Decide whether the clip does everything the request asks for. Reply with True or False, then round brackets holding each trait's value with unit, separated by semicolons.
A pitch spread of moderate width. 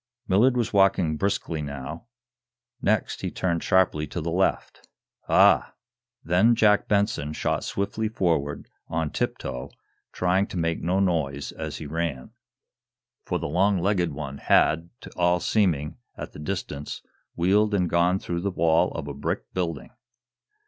True (4.0 semitones)